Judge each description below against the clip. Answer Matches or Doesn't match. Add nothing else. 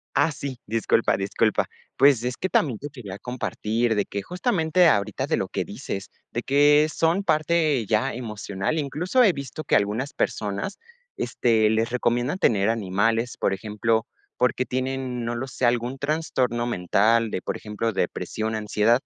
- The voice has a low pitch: Matches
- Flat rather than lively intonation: Doesn't match